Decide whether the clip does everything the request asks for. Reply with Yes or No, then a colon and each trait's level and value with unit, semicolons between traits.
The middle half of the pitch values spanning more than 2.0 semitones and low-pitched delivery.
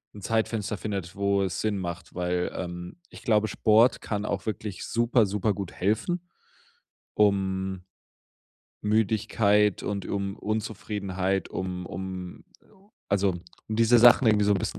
Yes: narrow, 2.4 semitones; low, 100 Hz